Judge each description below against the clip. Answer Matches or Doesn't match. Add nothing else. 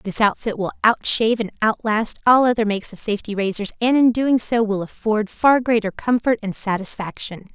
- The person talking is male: Doesn't match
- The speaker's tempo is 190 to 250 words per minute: Matches